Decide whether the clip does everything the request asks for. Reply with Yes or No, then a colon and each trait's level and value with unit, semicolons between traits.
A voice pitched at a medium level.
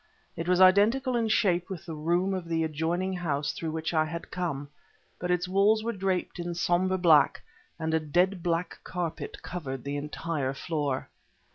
Yes: medium, 175 Hz